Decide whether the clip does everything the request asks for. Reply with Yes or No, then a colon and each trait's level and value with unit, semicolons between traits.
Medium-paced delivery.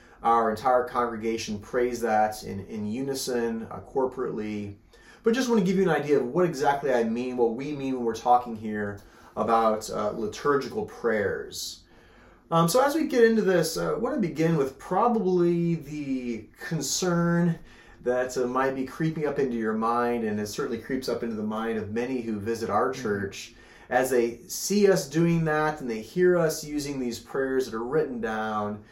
Yes: average, 185 wpm